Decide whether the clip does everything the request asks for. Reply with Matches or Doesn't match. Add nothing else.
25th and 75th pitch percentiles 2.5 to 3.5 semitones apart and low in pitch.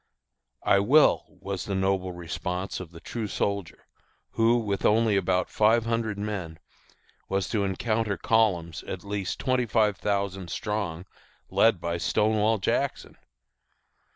Matches